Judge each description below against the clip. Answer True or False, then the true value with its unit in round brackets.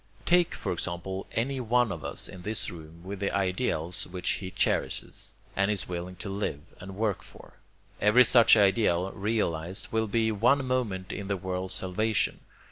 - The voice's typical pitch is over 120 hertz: False (100 Hz)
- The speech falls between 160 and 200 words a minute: True (170 wpm)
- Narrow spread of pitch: False (3.5 semitones)